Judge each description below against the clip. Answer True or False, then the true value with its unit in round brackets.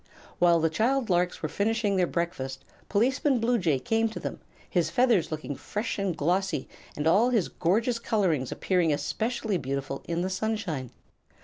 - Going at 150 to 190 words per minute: True (155 wpm)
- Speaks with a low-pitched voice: False (185 Hz)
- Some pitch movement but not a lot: False (5.7 semitones)